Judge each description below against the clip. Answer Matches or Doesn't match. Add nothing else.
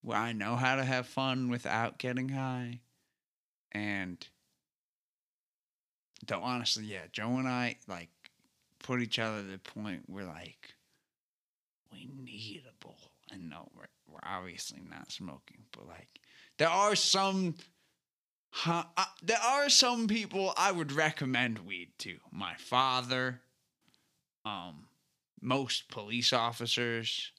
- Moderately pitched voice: Doesn't match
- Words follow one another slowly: Matches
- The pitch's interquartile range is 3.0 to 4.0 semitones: Doesn't match